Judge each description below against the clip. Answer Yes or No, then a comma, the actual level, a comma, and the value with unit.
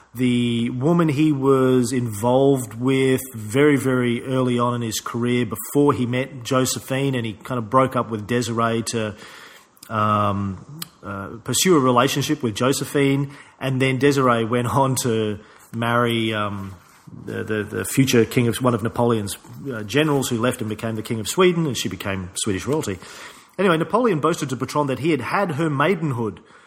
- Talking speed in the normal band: Yes, average, 170 wpm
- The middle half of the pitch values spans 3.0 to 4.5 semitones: Yes, average, 3.3 semitones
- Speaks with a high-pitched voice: No, low, 125 Hz